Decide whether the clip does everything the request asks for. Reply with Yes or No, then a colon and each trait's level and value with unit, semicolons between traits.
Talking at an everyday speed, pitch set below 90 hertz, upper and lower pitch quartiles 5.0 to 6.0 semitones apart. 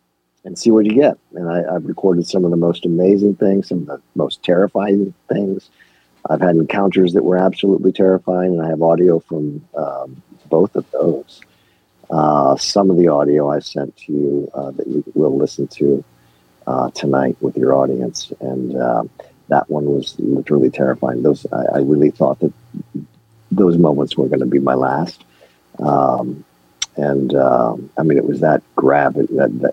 Yes: average, 180 wpm; very low, 75 Hz; average, 5.3 semitones